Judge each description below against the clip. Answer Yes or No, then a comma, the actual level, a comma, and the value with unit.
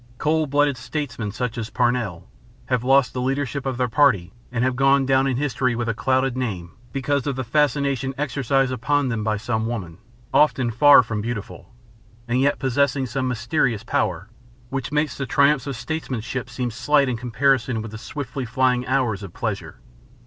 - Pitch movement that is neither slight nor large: Yes, average, 3.0 semitones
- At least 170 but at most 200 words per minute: Yes, average, 180 wpm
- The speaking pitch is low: Yes, low, 130 Hz